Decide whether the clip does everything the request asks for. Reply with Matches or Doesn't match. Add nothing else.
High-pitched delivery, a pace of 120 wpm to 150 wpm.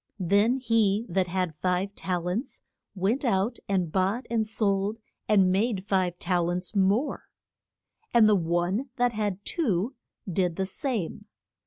Matches